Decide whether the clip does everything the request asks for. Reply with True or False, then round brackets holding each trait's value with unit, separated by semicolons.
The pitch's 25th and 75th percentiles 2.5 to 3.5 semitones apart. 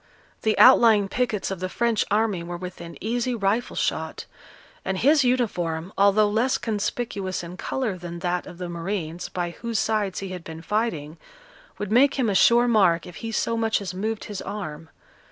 False (4.3 semitones)